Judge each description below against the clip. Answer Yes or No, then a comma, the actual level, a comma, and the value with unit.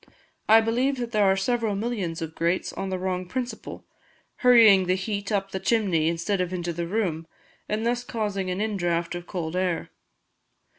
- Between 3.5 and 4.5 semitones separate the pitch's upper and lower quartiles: Yes, average, 4.0 semitones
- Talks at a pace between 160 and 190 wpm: Yes, average, 185 wpm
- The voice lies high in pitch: Yes, high, 195 Hz